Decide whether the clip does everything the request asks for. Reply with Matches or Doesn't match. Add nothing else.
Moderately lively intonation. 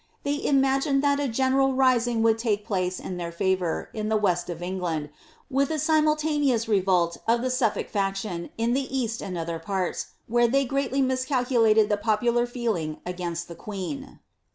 Doesn't match